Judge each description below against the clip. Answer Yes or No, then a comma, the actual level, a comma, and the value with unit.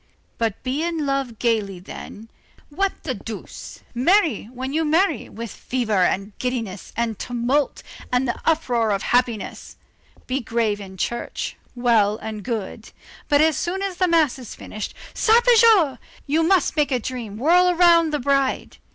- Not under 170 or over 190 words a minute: No, average, 155 wpm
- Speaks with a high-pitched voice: Yes, very high, 255 Hz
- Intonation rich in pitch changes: Yes, wide, 6.2 semitones